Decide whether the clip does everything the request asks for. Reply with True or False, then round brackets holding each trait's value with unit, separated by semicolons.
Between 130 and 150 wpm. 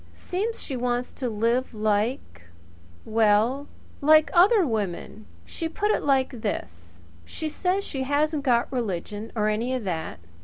True (145 wpm)